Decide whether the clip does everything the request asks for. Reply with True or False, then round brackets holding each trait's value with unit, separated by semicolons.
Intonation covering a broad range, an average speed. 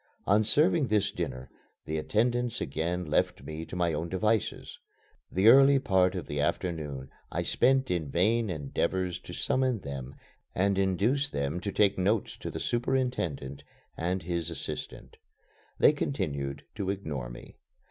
True (6.4 semitones; 145 wpm)